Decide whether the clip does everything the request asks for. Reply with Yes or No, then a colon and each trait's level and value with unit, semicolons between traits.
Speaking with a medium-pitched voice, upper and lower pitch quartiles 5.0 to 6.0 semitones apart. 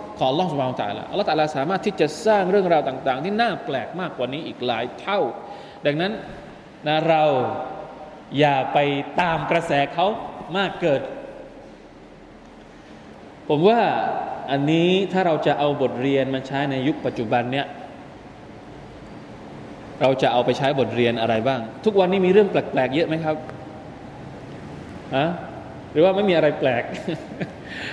Yes: medium, 150 Hz; wide, 5.4 semitones